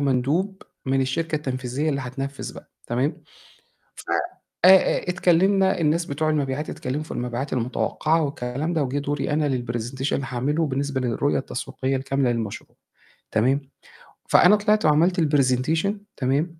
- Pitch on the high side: No, medium, 140 Hz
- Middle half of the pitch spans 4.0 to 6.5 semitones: No, average, 3.5 semitones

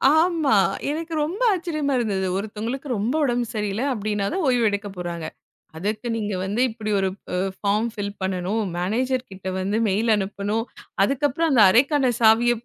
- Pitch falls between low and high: No, high, 220 Hz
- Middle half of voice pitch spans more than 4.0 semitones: Yes, average, 4.6 semitones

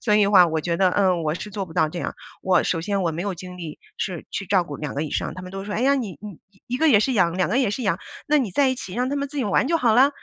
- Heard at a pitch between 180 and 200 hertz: Yes, high, 195 Hz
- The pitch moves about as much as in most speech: No, wide, 5.7 semitones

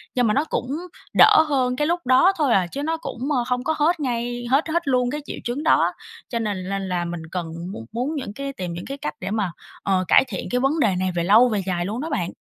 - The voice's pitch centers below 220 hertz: No, high, 245 Hz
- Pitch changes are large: Yes, wide, 6.8 semitones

